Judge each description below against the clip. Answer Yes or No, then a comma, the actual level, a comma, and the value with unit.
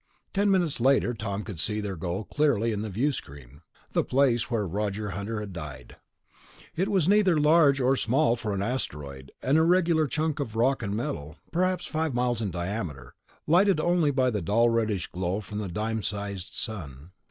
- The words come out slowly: No, average, 180 wpm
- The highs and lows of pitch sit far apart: Yes, wide, 7.0 semitones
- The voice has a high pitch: No, low, 110 Hz